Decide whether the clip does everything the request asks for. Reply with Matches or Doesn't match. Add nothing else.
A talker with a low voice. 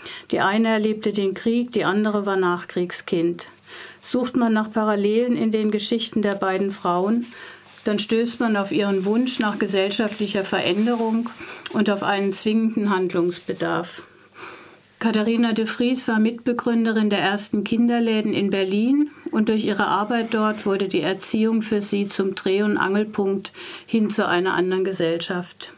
Doesn't match